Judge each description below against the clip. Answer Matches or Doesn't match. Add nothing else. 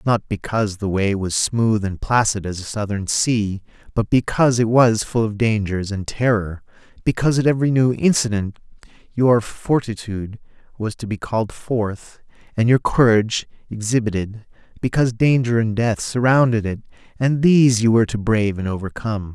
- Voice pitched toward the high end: Doesn't match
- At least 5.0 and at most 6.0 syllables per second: Matches